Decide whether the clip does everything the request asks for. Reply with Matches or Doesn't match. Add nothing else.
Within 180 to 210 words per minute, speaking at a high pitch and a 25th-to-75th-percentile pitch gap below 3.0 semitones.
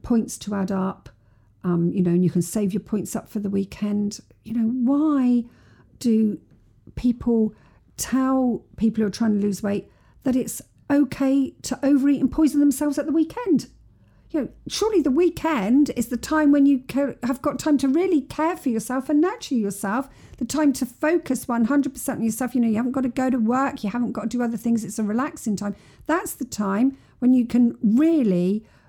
Doesn't match